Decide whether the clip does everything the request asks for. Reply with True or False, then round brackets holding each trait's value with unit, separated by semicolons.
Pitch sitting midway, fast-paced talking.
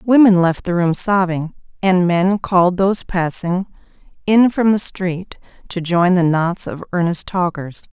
False (180 Hz; 160 wpm)